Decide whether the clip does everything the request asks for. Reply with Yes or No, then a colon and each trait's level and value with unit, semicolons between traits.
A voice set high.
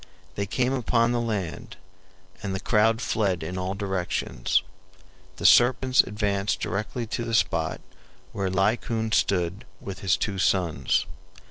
No: low, 100 Hz